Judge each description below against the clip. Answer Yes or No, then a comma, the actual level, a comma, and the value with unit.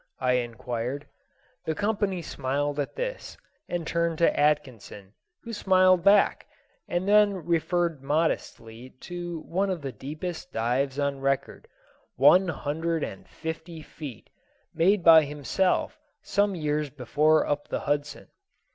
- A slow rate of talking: Yes, slow, 130 wpm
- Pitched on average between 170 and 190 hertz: No, medium, 155 Hz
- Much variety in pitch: No, average, 4.2 semitones